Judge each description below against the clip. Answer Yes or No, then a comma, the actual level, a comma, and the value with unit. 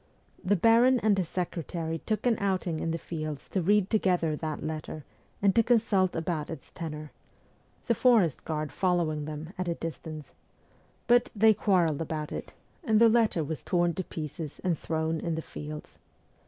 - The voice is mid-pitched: Yes, medium, 170 Hz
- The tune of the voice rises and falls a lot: No, average, 4.4 semitones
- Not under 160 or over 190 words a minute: Yes, average, 170 wpm